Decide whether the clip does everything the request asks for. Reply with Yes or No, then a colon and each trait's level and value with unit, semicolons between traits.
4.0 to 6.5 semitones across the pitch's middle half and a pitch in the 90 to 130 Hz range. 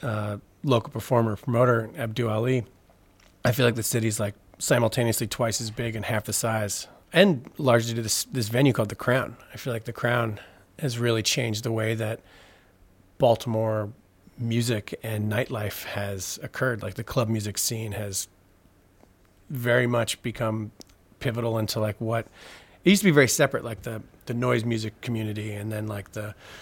No: narrow, 2.5 semitones; low, 110 Hz